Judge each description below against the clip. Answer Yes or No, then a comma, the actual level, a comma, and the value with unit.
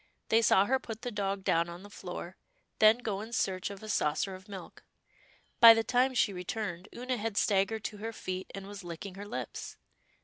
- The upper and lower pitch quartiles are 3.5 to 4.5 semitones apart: No, average, 3.0 semitones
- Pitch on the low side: No, high, 205 Hz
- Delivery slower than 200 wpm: No, fast, 205 wpm